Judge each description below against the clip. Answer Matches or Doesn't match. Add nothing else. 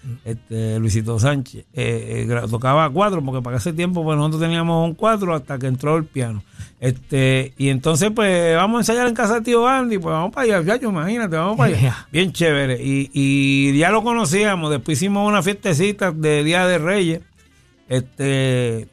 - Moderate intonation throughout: Doesn't match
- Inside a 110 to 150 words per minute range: Doesn't match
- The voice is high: Doesn't match